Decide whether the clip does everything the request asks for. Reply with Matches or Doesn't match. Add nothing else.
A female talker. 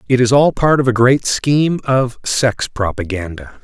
Doesn't match